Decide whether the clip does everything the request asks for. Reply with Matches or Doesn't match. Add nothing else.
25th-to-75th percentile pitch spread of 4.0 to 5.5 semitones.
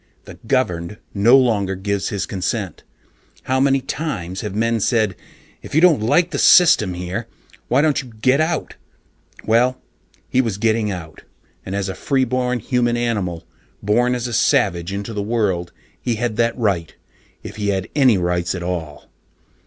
Matches